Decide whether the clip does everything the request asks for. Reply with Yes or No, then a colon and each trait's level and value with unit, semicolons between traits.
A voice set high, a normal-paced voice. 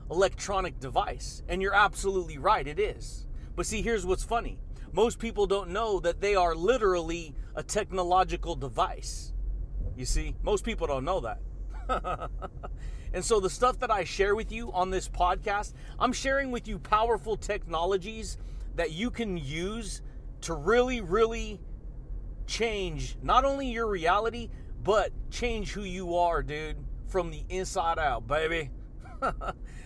Yes: high, 195 Hz; average, 145 wpm